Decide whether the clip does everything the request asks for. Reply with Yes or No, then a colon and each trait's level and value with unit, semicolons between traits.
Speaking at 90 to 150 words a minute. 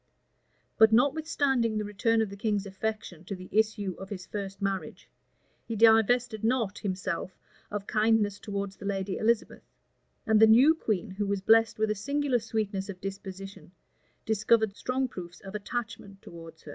No: average, 160 wpm